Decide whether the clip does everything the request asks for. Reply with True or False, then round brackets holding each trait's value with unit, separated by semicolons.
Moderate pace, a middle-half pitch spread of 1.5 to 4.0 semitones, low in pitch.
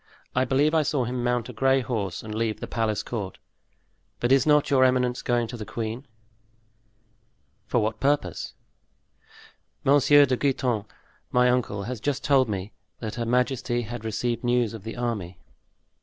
True (165 wpm; 2.8 semitones; 120 Hz)